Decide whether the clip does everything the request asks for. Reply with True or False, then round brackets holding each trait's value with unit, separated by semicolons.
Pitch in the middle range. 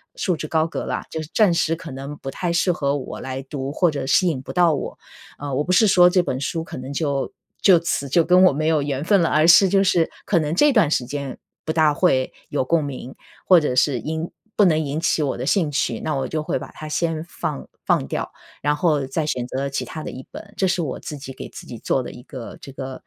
True (155 Hz)